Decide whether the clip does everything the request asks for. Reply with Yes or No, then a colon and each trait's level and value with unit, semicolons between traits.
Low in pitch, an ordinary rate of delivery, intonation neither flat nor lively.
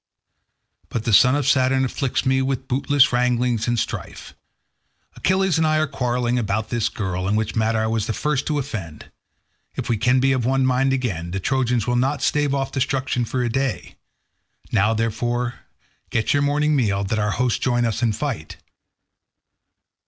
Yes: low, 125 Hz; average, 175 wpm; average, 3.1 semitones